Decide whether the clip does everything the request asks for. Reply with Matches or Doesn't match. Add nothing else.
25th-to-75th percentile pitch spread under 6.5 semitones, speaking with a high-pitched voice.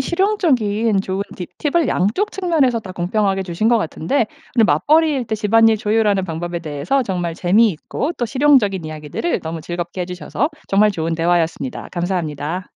Matches